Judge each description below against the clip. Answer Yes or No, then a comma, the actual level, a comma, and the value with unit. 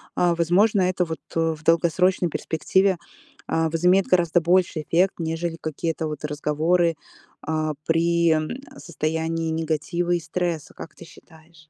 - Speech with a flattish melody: Yes, narrow, 1.7 semitones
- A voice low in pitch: No, medium, 165 Hz